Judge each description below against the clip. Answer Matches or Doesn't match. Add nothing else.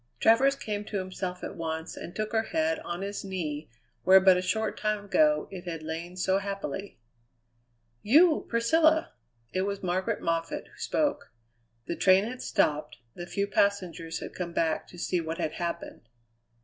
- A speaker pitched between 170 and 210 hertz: Matches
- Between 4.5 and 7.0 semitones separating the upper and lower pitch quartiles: Doesn't match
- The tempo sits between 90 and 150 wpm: Doesn't match